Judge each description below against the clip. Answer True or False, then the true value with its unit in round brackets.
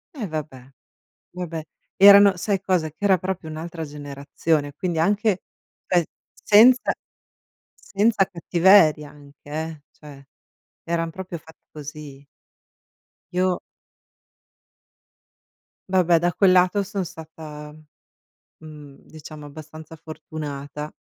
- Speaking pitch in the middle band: True (160 Hz)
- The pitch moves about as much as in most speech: True (3.7 semitones)